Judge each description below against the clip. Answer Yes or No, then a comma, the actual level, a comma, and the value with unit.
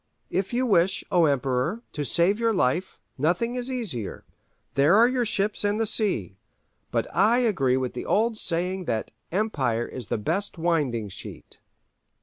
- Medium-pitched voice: Yes, medium, 180 Hz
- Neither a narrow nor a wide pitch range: No, wide, 8.7 semitones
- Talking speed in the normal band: Yes, average, 160 wpm